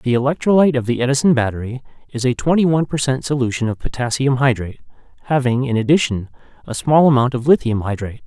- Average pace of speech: Yes, average, 180 wpm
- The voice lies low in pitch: Yes, low, 130 Hz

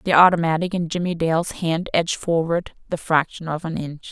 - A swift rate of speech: No, average, 190 wpm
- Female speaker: Yes, female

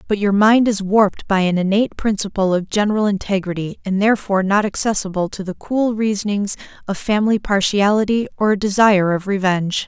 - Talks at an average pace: Yes, average, 170 wpm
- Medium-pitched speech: No, high, 200 Hz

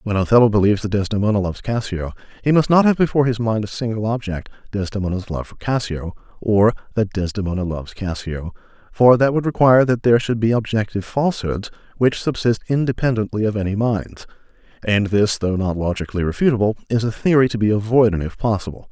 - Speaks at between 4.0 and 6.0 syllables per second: No, 6.3 syllables/s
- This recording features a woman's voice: No, male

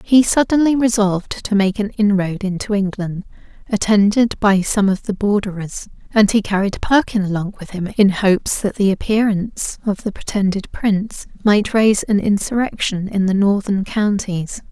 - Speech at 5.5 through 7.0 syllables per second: No, 4.9 syllables/s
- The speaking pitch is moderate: No, high, 205 Hz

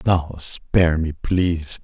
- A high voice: No, very low, 85 Hz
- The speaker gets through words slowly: Yes, slow, 130 wpm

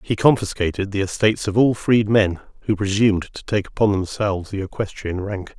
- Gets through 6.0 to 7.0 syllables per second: No, 5.6 syllables/s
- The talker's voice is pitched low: Yes, low, 100 Hz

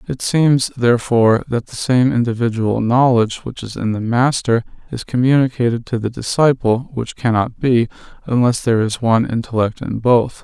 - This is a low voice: Yes, low, 120 Hz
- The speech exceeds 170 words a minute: No, average, 160 wpm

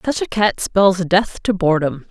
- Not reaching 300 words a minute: Yes, average, 200 wpm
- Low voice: No, high, 195 Hz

